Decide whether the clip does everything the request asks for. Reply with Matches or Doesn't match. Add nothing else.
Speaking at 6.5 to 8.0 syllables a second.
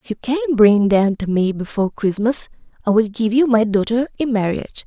Doesn't match